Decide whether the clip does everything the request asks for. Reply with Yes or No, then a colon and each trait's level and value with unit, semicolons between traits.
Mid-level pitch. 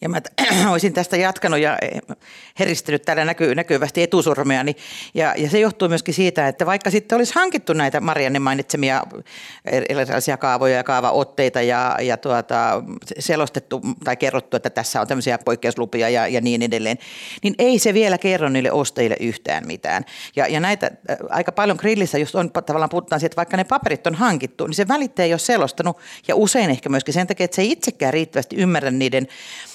Yes: medium, 165 Hz